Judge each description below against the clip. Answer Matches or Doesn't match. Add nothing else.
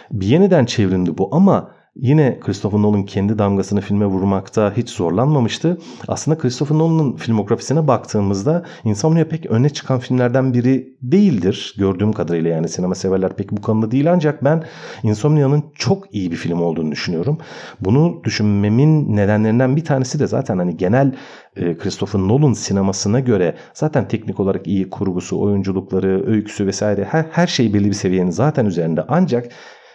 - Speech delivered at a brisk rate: Matches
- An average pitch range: Doesn't match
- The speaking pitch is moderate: Doesn't match